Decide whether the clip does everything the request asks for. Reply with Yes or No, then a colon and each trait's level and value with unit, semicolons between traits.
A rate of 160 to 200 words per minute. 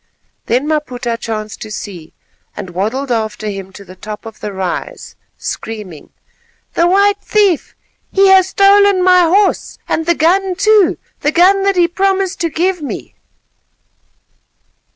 No: average, 145 wpm